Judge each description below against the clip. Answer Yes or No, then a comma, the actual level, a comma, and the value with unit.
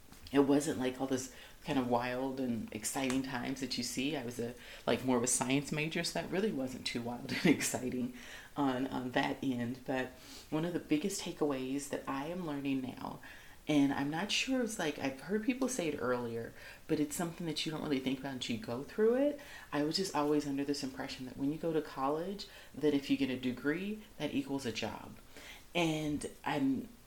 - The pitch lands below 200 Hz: Yes, medium, 140 Hz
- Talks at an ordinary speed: No, fast, 215 wpm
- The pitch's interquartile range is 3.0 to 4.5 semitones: Yes, average, 3.6 semitones